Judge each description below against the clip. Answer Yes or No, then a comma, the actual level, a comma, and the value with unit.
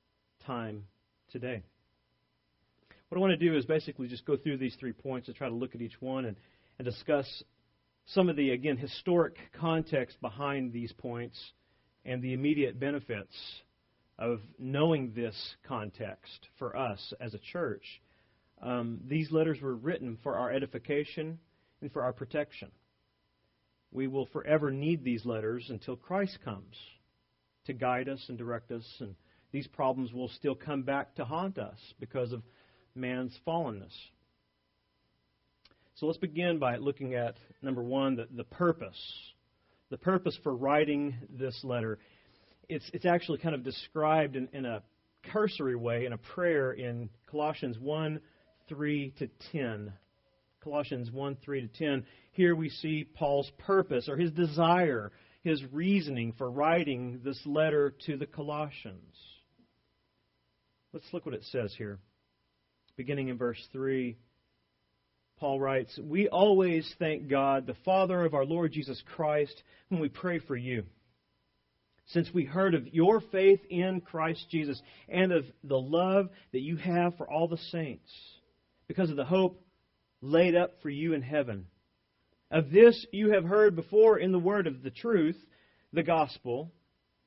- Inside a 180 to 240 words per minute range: No, average, 150 wpm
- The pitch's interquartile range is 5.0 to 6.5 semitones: Yes, wide, 5.5 semitones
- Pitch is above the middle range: No, low, 135 Hz